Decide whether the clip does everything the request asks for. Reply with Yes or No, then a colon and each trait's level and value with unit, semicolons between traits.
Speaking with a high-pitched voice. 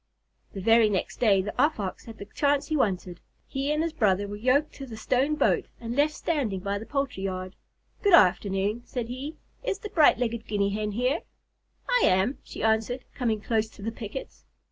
Yes: high, 225 Hz